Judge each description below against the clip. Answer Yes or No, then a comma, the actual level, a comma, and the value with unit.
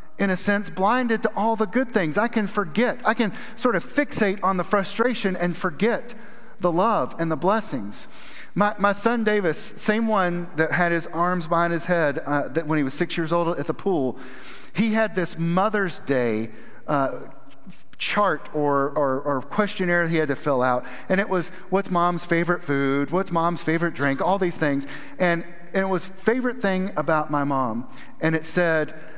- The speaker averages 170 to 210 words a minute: Yes, average, 190 wpm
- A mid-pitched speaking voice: Yes, medium, 175 Hz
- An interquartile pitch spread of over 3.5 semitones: Yes, average, 4.5 semitones